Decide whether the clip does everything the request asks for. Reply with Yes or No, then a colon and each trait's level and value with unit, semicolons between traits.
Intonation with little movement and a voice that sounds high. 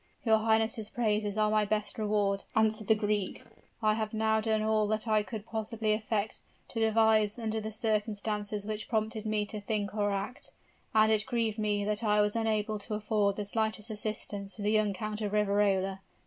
Yes: narrow, 0.9 semitones; high, 215 Hz